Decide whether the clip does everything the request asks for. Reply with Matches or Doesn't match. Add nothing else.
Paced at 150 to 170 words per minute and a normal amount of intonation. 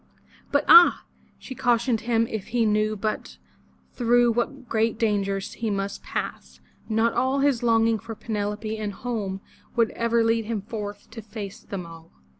Doesn't match